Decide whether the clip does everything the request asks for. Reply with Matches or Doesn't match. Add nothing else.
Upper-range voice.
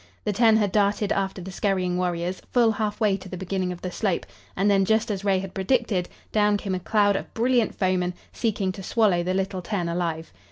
Matches